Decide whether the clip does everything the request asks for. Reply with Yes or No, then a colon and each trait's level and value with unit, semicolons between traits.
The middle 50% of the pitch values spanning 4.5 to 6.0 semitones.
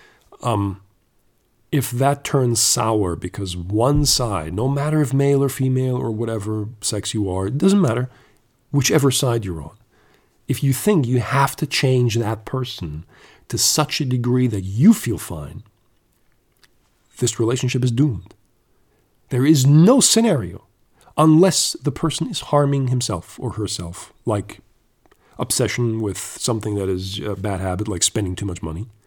Yes: average, 4.8 semitones